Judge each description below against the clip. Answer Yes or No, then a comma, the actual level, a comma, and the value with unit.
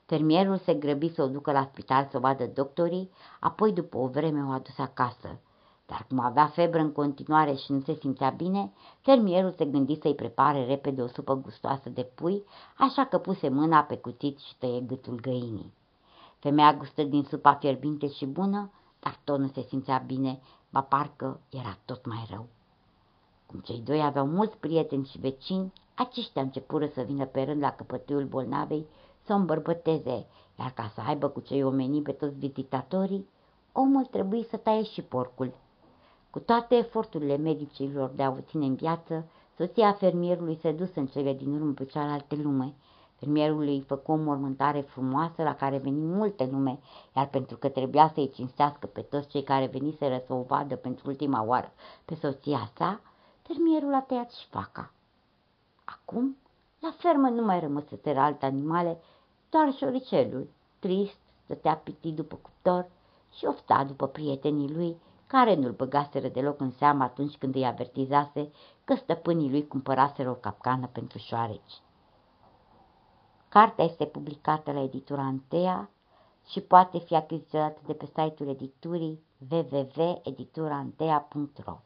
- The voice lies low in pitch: No, medium, 145 Hz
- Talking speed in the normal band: Yes, average, 160 wpm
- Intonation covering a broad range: No, average, 3.5 semitones